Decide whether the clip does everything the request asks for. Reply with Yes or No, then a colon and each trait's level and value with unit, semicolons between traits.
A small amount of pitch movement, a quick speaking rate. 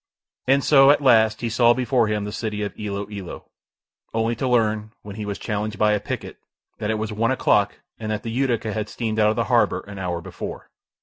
Yes: narrow, 2.1 semitones; fast, 225 wpm